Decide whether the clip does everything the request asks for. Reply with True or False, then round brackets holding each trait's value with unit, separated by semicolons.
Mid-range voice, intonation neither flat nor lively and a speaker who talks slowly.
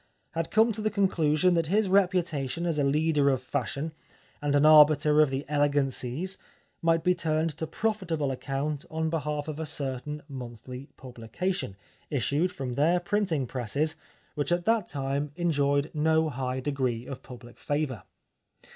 False (150 Hz; 3.4 semitones; 160 wpm)